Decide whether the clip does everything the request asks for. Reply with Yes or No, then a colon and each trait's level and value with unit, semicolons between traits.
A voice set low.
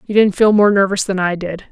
No: high, 195 Hz